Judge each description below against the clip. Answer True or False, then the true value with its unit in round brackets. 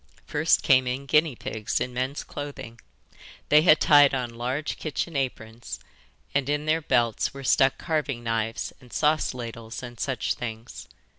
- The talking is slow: False (155 wpm)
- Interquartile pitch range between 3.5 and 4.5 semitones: True (3.8 semitones)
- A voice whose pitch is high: False (130 Hz)